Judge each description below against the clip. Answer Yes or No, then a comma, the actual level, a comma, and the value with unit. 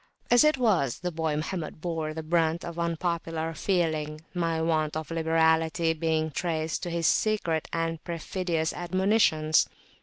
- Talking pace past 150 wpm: No, average, 145 wpm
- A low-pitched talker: No, medium, 165 Hz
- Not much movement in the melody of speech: Yes, narrow, 1.5 semitones